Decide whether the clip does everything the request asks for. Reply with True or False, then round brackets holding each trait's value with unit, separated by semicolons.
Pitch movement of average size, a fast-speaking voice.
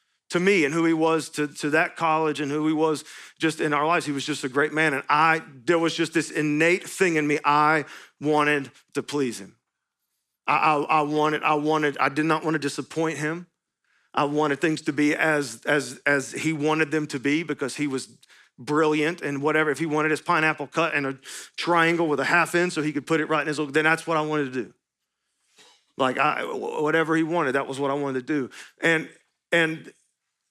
False (1.7 semitones; 220 wpm)